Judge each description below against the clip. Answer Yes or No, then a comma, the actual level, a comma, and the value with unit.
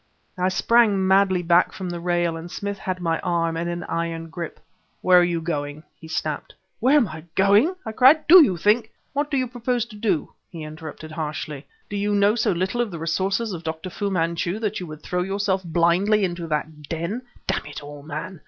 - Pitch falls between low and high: Yes, medium, 180 Hz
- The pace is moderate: No, fast, 215 wpm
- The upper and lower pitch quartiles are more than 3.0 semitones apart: Yes, average, 3.9 semitones